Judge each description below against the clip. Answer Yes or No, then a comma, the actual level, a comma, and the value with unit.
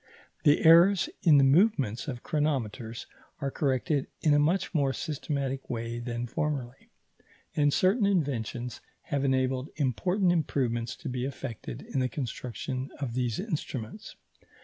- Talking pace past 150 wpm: No, slow, 135 wpm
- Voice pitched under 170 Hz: Yes, low, 135 Hz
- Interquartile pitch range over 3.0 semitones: Yes, average, 3.8 semitones